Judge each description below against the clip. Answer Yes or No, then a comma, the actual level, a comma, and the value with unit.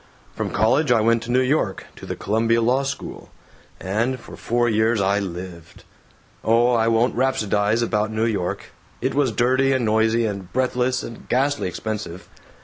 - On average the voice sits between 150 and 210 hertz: No, low, 115 Hz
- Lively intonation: No, average, 2.9 semitones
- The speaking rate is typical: Yes, average, 165 wpm